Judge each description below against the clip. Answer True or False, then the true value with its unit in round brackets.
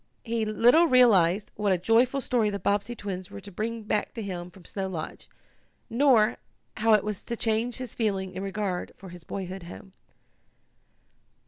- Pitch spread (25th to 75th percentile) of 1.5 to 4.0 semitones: True (3.3 semitones)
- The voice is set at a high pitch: True (210 Hz)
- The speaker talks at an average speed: True (175 wpm)